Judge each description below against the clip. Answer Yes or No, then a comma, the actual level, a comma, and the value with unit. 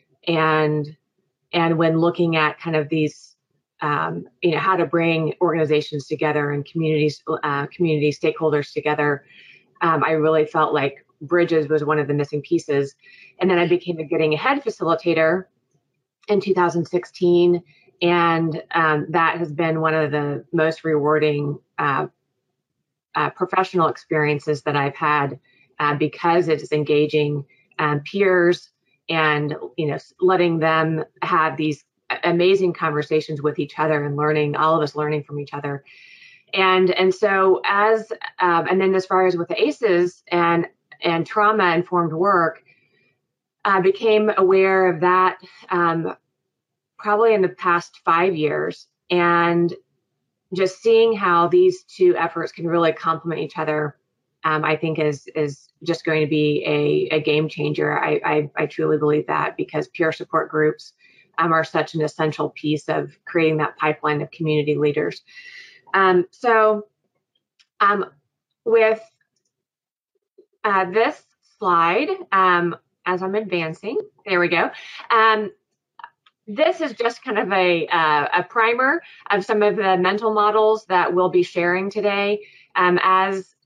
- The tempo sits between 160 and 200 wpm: No, average, 145 wpm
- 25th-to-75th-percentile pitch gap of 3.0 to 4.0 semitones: Yes, average, 3.7 semitones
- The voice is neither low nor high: Yes, medium, 170 Hz